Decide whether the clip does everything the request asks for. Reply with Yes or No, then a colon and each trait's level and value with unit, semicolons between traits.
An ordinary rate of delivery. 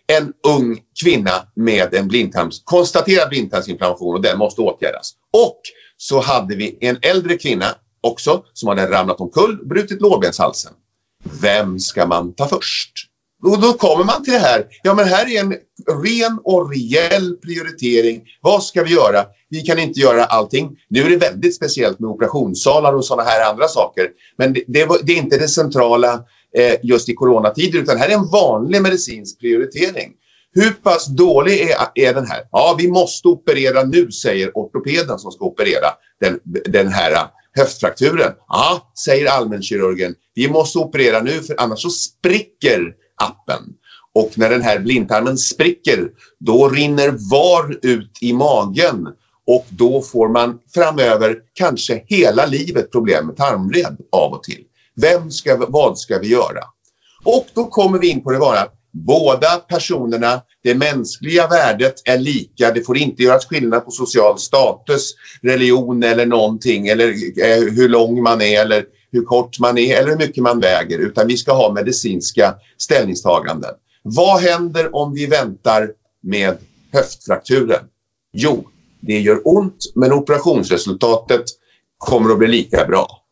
Yes: average, 155 wpm